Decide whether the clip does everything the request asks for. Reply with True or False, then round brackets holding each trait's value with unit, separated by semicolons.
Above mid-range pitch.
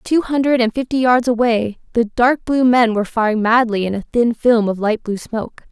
True (235 Hz)